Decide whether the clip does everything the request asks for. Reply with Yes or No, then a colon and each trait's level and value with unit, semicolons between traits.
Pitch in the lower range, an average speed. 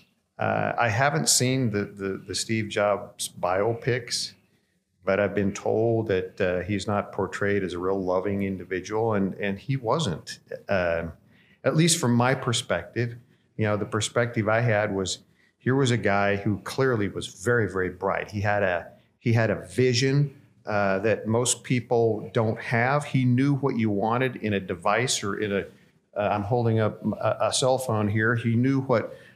Yes: low, 110 Hz; average, 180 wpm